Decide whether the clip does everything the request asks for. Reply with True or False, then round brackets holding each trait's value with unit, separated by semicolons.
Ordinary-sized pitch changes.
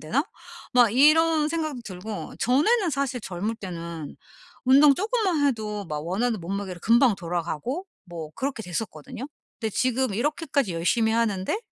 False (7.2 semitones)